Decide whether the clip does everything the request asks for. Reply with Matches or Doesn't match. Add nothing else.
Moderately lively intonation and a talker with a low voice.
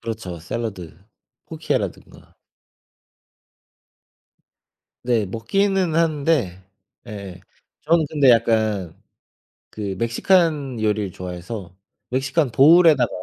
Doesn't match